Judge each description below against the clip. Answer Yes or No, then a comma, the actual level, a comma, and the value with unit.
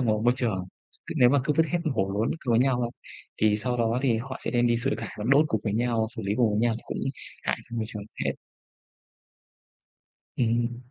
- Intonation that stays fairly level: Yes, narrow, 2.2 semitones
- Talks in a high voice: No, low, 120 Hz